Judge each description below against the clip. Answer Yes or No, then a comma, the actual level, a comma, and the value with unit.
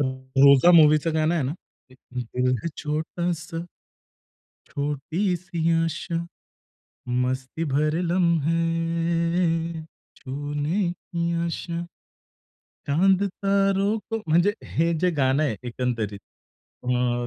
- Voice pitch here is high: No, medium, 165 Hz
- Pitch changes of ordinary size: Yes, average, 3.5 semitones